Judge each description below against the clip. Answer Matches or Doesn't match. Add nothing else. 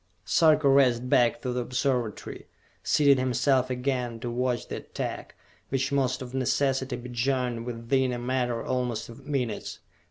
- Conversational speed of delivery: Matches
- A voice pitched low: Matches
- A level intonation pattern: Matches